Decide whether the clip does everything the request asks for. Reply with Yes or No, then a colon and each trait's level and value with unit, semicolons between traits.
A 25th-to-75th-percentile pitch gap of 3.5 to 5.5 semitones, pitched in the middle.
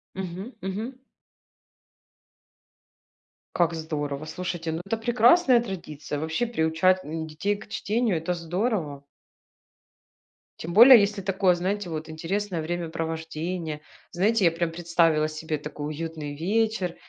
Yes: average, 4.2 semitones; medium, 175 Hz